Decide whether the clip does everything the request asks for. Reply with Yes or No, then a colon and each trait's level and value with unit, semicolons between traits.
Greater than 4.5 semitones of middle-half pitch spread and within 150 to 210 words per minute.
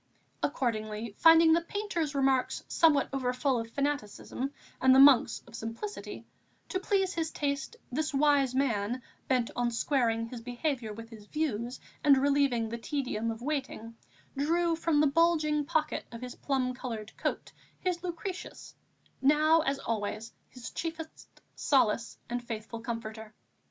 No: average, 4.9 semitones; average, 140 wpm